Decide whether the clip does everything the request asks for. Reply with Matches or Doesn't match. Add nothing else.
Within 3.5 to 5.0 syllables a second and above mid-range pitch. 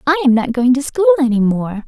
Doesn't match